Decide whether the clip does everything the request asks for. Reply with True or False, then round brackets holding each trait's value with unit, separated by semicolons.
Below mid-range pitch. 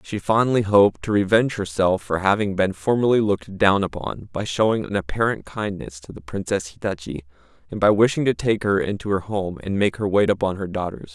True (100 Hz)